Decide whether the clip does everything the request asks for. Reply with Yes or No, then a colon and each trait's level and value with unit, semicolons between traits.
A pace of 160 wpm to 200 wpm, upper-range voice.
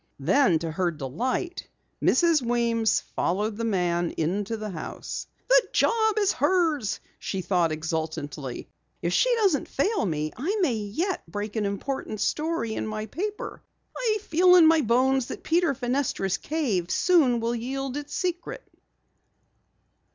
No: average, 145 wpm; high, 235 Hz